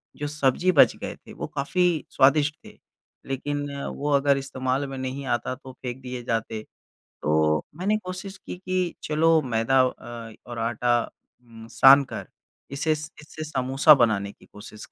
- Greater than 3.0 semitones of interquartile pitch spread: Yes, average, 4.0 semitones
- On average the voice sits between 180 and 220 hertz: No, low, 135 Hz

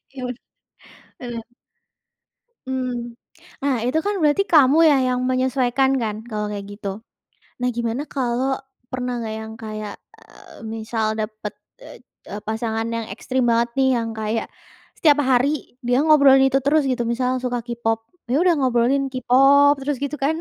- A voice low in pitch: No, very high, 250 Hz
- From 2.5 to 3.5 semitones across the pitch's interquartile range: Yes, average, 2.9 semitones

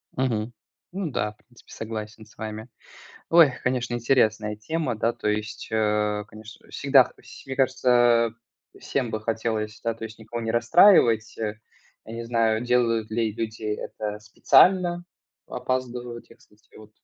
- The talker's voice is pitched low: Yes, low, 115 Hz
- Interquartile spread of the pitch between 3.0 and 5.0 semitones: No, narrow, 2.4 semitones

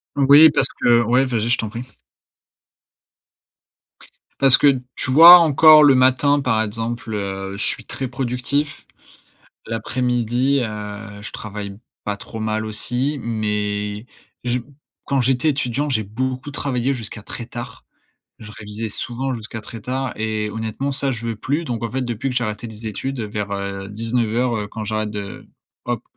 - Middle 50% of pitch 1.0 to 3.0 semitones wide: No, average, 3.5 semitones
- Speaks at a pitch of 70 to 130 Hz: Yes, low, 115 Hz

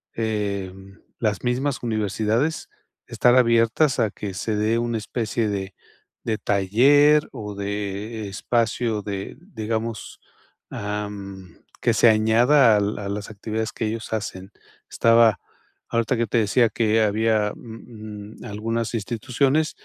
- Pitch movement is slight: Yes, narrow, 2.2 semitones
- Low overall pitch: Yes, low, 110 Hz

